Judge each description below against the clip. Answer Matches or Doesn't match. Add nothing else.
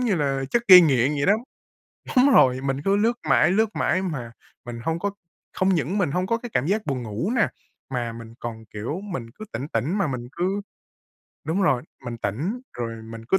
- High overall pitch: Doesn't match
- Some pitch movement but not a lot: Doesn't match